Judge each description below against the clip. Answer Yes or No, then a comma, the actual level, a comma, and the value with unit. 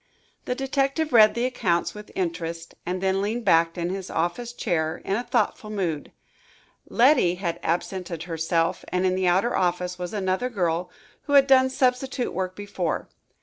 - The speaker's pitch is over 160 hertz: Yes, high, 190 Hz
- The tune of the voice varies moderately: No, wide, 5.7 semitones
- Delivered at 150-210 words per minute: Yes, average, 165 wpm